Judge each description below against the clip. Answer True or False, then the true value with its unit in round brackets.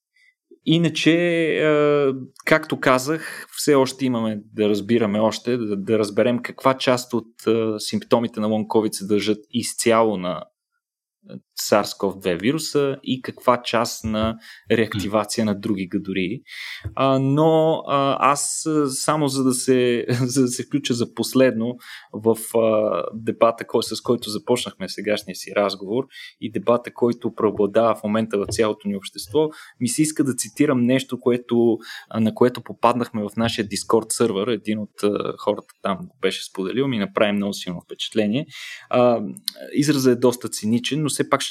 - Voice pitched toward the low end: True (120 Hz)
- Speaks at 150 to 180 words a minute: False (135 wpm)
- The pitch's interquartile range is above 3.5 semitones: True (4.1 semitones)